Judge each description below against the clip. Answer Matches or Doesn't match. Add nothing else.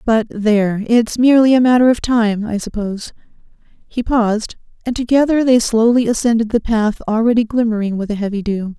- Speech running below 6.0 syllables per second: Matches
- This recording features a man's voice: Doesn't match